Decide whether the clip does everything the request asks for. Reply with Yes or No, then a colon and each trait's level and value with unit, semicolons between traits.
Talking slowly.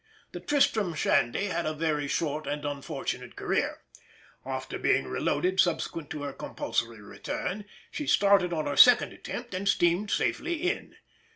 No: average, 150 wpm